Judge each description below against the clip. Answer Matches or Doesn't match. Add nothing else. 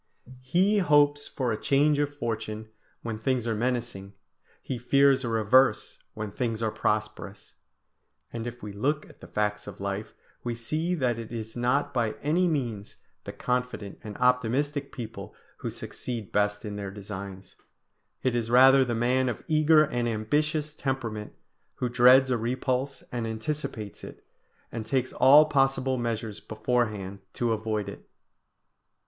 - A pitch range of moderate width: Matches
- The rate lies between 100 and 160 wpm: Matches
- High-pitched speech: Doesn't match